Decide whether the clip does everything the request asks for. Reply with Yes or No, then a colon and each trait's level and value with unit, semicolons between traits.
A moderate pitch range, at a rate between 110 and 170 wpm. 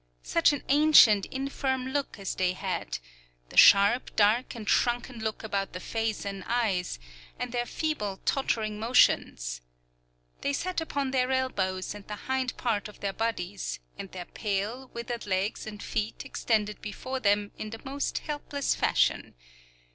Yes: average, 4.5 semitones; average, 155 wpm